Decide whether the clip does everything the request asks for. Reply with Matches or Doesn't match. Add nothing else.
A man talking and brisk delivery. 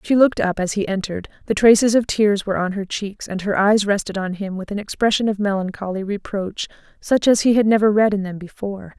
Doesn't match